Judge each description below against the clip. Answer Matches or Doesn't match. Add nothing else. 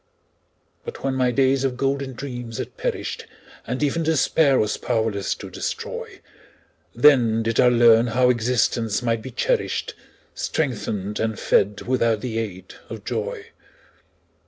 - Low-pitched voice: Matches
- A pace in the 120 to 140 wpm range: Matches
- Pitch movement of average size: Matches